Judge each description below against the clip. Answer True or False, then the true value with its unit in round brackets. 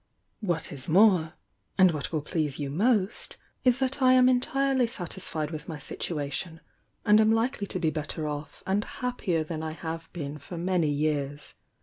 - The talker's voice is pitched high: False (170 Hz)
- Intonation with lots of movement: True (6.1 semitones)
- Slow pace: False (185 wpm)